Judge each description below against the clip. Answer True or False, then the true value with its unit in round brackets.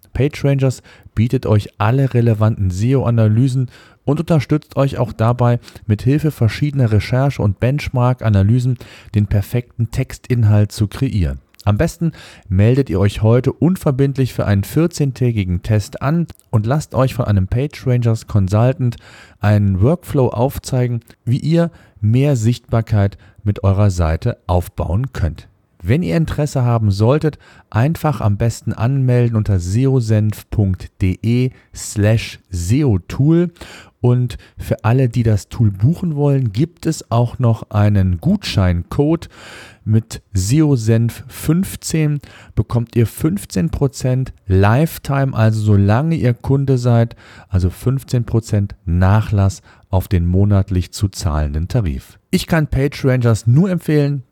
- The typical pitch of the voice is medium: False (115 Hz)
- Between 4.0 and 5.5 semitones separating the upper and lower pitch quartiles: True (4.5 semitones)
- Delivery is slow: True (115 wpm)